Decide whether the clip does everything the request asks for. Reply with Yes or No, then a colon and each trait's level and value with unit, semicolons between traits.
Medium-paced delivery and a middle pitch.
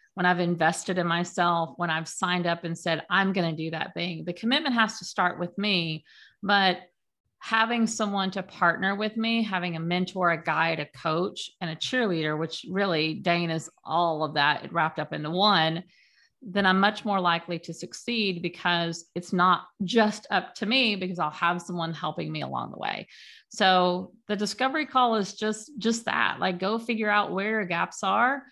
Yes: average, 190 wpm; medium, 180 Hz